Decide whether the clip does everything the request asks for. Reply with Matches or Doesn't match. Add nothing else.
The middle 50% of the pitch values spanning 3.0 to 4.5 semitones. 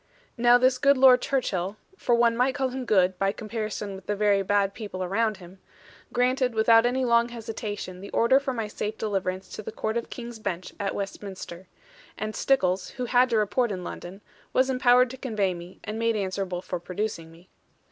Matches